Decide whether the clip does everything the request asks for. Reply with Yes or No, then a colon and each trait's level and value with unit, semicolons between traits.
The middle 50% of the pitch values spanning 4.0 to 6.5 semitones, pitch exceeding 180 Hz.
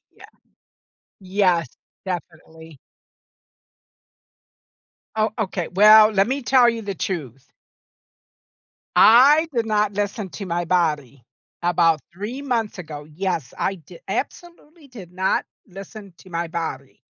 Yes: average, 4.6 semitones; high, 190 Hz